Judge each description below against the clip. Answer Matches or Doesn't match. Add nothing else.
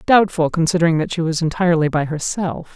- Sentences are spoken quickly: Doesn't match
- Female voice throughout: Matches